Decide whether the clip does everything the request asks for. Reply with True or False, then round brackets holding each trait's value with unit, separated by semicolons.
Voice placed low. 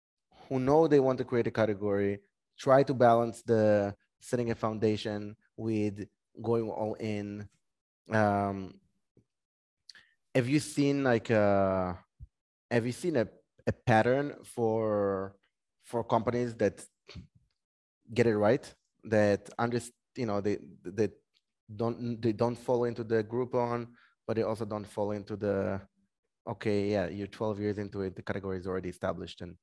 True (110 Hz)